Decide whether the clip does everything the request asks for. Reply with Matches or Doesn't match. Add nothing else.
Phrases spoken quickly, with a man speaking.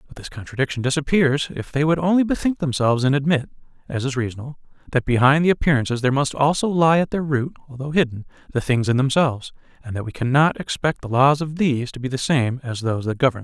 Matches